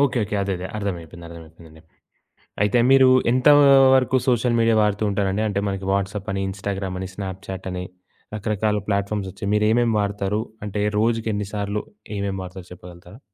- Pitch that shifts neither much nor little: No, narrow, 2.1 semitones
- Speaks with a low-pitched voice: Yes, low, 100 Hz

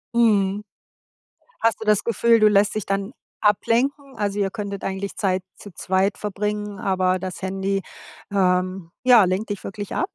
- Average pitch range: No, narrow, 1.9 semitones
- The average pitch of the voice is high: Yes, high, 200 Hz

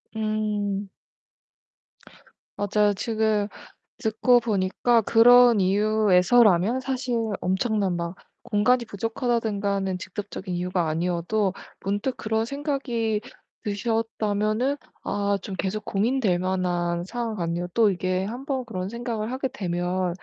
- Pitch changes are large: No, average, 3.7 semitones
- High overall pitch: Yes, high, 210 Hz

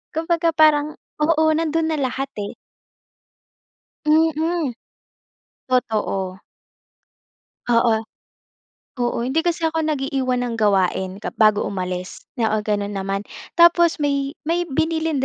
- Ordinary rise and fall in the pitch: No, wide, 6.8 semitones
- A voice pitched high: Yes, very high, 275 Hz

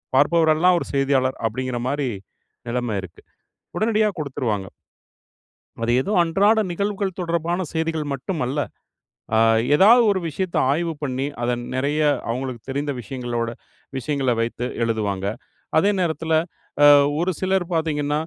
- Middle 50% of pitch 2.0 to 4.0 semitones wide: No, average, 5.3 semitones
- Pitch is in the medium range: Yes, medium, 145 Hz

